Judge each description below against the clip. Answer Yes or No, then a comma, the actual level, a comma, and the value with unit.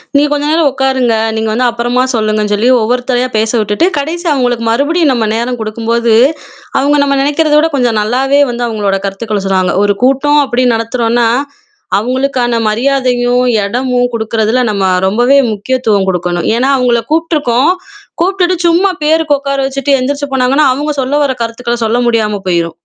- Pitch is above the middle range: Yes, high, 245 Hz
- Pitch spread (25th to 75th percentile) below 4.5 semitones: Yes, average, 3.9 semitones